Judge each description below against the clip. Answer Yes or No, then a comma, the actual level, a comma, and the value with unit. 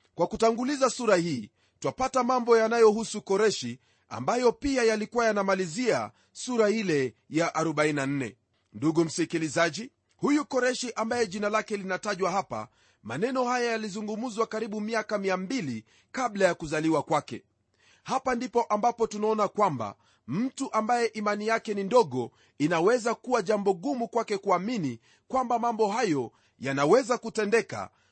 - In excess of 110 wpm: Yes, average, 120 wpm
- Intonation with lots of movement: Yes, wide, 6.1 semitones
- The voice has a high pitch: Yes, high, 215 Hz